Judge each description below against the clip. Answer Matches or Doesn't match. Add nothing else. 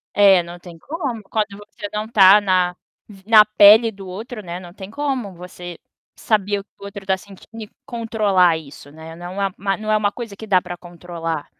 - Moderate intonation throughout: Matches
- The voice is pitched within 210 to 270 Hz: Doesn't match